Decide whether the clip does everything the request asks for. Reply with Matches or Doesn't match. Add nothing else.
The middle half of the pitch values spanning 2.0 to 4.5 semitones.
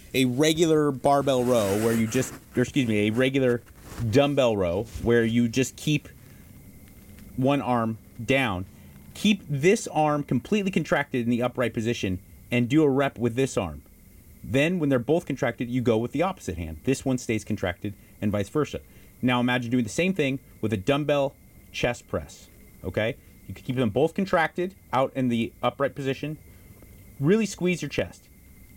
Doesn't match